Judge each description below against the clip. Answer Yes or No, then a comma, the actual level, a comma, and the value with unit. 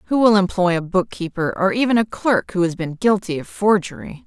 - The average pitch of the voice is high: Yes, high, 195 Hz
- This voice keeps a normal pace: No, fast, 210 wpm